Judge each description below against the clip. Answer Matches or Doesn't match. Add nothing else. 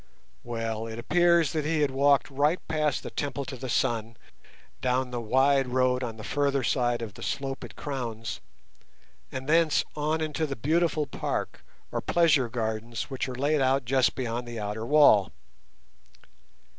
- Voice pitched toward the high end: Doesn't match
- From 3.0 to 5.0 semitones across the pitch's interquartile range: Matches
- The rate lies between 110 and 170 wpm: Matches